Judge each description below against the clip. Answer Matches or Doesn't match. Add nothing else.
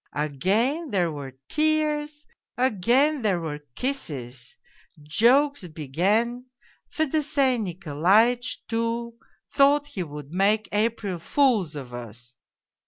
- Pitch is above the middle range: Matches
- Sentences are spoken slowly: Matches